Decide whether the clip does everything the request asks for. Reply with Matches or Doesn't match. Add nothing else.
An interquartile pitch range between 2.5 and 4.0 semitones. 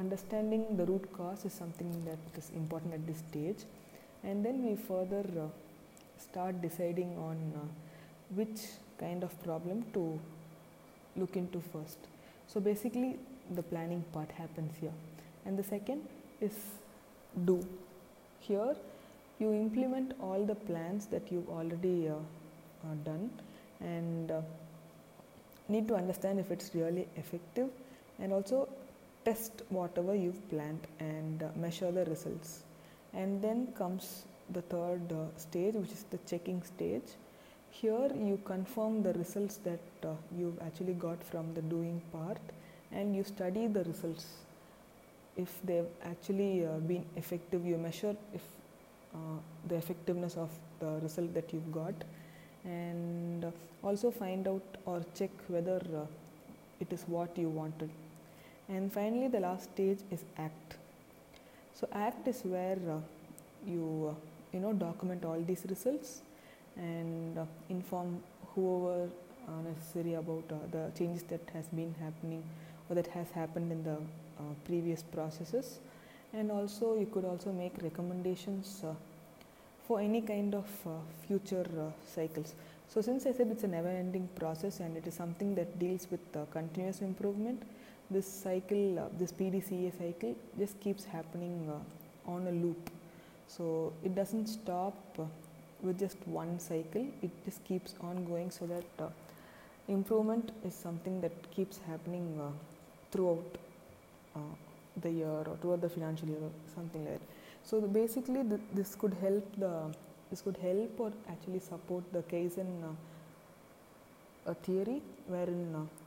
Matches